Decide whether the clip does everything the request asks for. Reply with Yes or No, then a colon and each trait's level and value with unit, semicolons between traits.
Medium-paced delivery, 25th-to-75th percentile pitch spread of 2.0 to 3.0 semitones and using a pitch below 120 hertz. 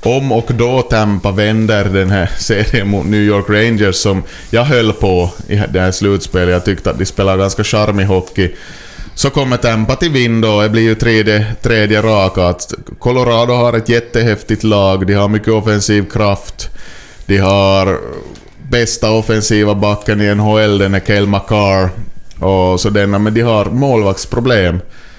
Yes: average, 160 wpm; narrow, 2.5 semitones; low, 105 Hz